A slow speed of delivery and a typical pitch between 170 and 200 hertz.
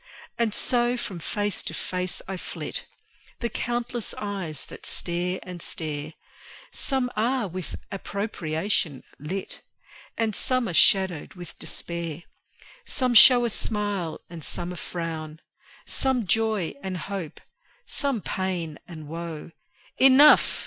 Yes: slow, 125 wpm; high, 190 Hz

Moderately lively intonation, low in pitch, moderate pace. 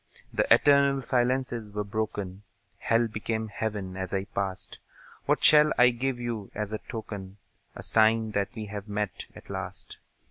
Yes: average, 3.0 semitones; low, 110 Hz; average, 155 wpm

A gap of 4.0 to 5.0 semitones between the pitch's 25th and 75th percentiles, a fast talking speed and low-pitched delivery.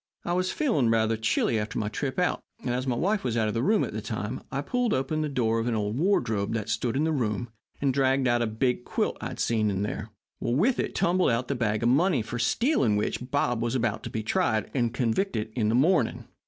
Yes: average, 4.3 semitones; fast, 245 wpm; low, 120 Hz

